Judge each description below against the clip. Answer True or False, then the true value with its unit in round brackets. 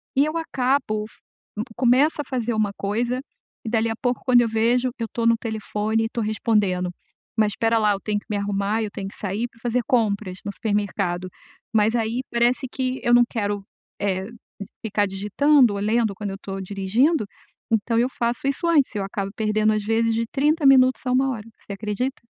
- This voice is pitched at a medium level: False (225 Hz)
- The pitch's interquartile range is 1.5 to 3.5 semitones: True (3.2 semitones)